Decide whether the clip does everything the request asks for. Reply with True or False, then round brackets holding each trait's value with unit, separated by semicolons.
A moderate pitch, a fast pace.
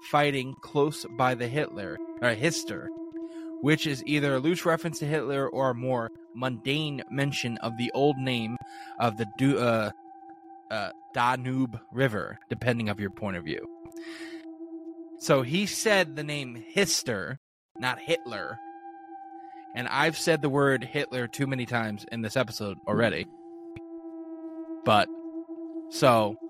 False (150 Hz; 135 wpm)